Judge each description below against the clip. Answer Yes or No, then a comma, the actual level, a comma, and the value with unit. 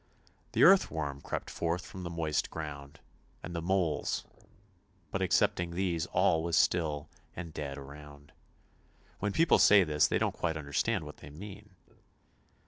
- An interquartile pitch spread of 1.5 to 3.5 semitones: No, average, 3.9 semitones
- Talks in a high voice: No, very low, 85 Hz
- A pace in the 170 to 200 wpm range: No, average, 155 wpm